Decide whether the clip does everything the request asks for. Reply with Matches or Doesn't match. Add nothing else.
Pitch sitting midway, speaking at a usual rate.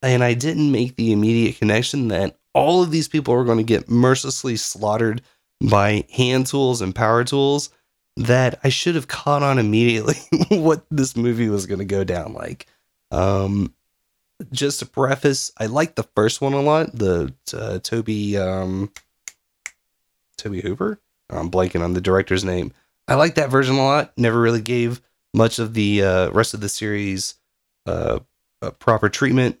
Doesn't match